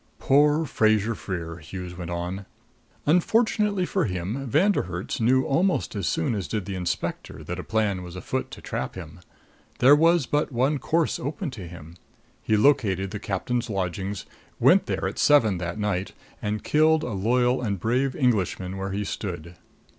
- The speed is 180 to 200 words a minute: No, average, 170 wpm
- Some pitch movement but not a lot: No, wide, 7.0 semitones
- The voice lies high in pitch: No, low, 105 Hz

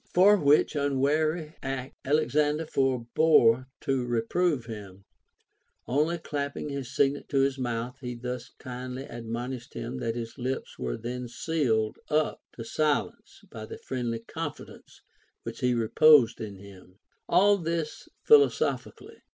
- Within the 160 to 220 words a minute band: No, slow, 135 wpm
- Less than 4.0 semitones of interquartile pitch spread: No, average, 4.3 semitones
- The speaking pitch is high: No, low, 130 Hz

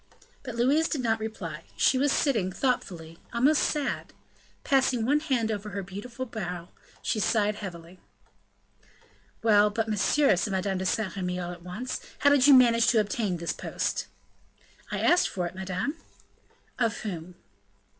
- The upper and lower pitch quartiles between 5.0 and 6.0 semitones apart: Yes, wide, 5.5 semitones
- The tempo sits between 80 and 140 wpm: No, average, 155 wpm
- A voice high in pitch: Yes, high, 215 Hz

